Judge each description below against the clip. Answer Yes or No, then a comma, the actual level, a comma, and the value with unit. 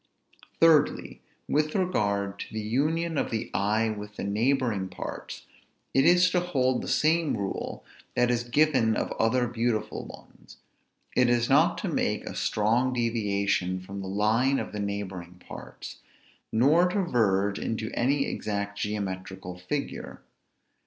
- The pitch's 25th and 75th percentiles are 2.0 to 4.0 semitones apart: No, average, 5.1 semitones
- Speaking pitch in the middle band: No, low, 115 Hz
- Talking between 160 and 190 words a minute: No, average, 145 wpm